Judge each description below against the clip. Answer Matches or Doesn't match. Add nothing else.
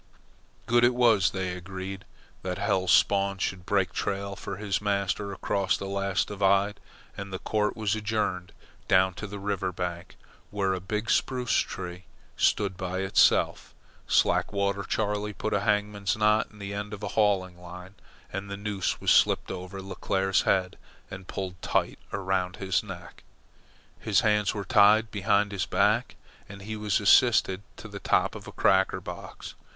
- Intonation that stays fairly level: Matches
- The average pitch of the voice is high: Doesn't match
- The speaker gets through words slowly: Doesn't match